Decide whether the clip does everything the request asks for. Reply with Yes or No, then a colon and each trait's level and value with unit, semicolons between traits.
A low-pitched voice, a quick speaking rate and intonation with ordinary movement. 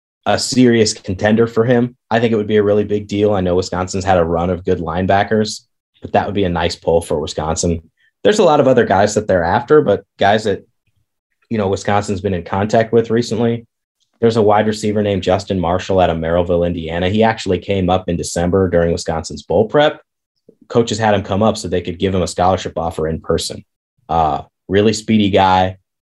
Yes: low, 100 Hz; fast, 210 wpm; average, 3.5 semitones